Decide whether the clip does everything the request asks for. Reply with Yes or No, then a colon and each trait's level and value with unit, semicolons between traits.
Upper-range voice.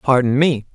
No: low, 130 Hz